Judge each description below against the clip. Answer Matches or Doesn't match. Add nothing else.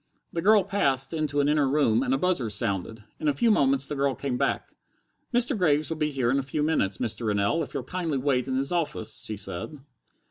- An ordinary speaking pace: Doesn't match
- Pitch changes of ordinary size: Matches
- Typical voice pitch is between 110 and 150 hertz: Matches